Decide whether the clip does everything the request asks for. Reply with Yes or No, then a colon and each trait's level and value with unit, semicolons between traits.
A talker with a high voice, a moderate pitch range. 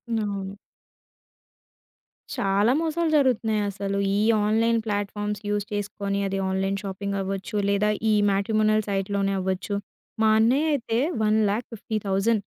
No: high, 205 Hz; narrow, 1.9 semitones